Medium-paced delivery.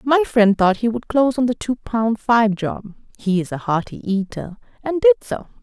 No: fast, 215 wpm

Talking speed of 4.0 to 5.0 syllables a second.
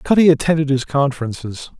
No: 6.1 syllables/s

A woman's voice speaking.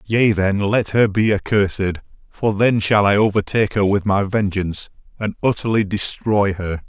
No: male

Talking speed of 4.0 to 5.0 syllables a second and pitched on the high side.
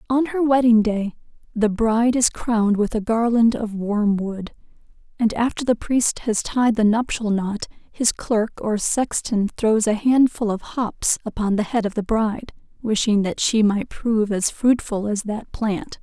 Yes: 4.4 syllables/s; high, 220 Hz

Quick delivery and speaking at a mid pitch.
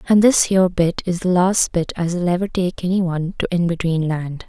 Yes: fast, 215 wpm; medium, 175 Hz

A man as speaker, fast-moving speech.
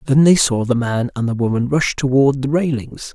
Yes: male; fast, 230 wpm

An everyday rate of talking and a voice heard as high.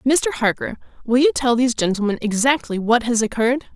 Yes: average, 175 wpm; high, 240 Hz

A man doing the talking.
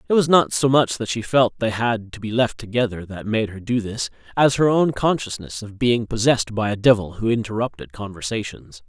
Yes: male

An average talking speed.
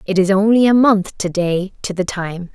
No: fast, 235 wpm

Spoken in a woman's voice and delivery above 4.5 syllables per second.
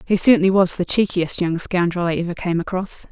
Yes: female; 5.7 syllables/s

